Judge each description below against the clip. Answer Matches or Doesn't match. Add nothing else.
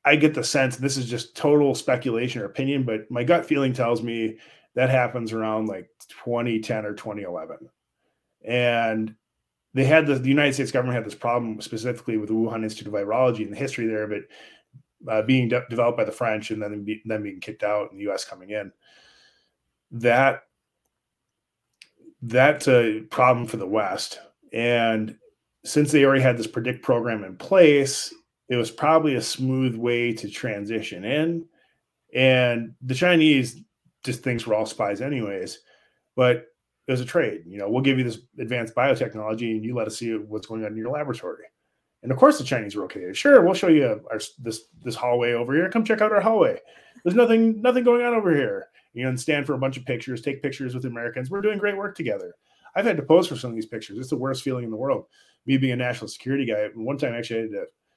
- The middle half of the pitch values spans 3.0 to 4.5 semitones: Matches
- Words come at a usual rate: Doesn't match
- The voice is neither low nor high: Doesn't match